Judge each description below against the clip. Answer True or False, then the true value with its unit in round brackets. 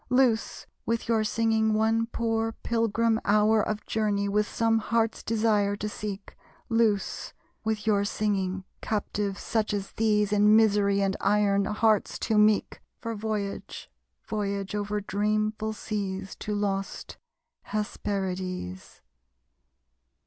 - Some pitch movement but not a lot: False (1.7 semitones)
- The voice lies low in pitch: False (210 Hz)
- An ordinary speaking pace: False (120 wpm)